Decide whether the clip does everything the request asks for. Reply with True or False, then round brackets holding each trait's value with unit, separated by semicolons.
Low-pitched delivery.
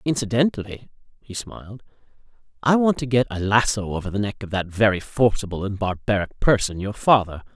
True (110 Hz)